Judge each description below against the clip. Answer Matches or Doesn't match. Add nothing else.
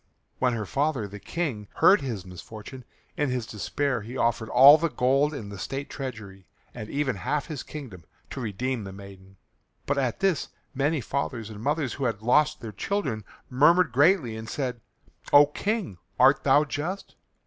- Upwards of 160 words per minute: Matches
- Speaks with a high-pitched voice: Doesn't match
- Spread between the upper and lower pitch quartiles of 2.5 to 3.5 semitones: Doesn't match